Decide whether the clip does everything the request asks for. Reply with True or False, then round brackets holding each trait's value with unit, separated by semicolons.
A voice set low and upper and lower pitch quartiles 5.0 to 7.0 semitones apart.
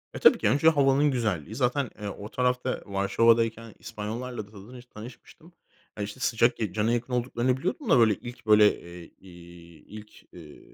False (115 Hz; 3.2 semitones)